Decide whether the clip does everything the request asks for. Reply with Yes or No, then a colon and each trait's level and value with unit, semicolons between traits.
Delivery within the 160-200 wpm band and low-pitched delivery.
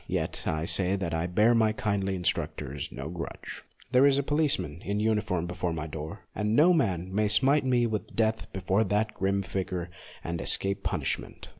Yes: average, 180 wpm; low, 100 Hz